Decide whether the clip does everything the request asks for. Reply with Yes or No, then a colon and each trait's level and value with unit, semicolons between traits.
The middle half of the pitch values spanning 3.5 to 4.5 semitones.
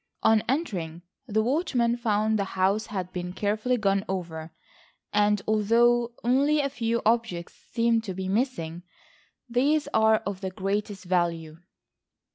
Yes: average, 4.0 semitones